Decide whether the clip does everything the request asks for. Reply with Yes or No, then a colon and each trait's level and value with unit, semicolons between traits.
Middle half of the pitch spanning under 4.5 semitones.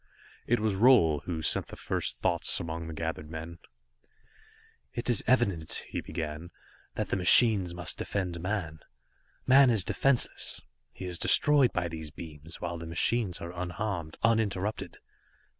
No: average, 5.0 semitones